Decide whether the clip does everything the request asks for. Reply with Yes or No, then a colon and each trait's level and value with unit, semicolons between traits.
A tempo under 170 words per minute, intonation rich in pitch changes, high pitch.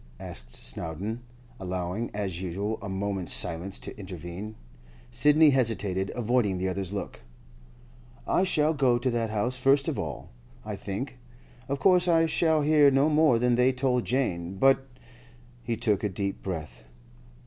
No: average, 150 wpm; wide, 6.0 semitones; low, 110 Hz